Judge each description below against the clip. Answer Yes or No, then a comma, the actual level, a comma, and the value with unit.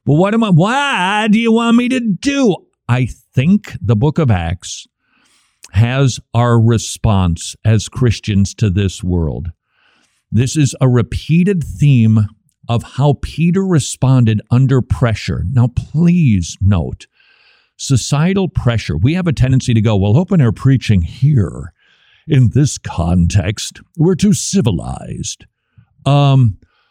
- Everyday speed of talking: No, slow, 130 wpm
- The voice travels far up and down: Yes, wide, 6.4 semitones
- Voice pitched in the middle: No, low, 125 Hz